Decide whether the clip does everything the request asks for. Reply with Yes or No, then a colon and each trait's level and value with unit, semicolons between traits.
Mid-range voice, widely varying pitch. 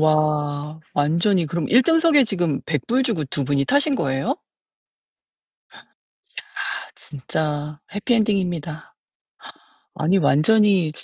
Yes: medium, 160 Hz; wide, 6.1 semitones